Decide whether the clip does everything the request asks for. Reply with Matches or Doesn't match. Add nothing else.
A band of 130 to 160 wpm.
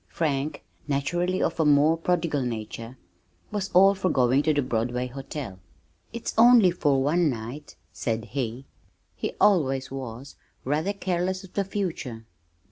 Matches